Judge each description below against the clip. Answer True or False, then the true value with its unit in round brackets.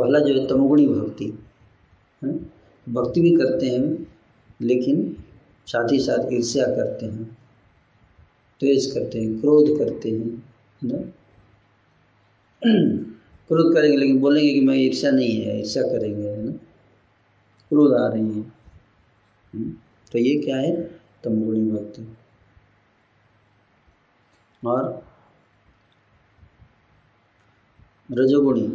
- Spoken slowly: True (105 wpm)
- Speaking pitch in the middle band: False (110 Hz)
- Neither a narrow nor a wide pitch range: True (4.2 semitones)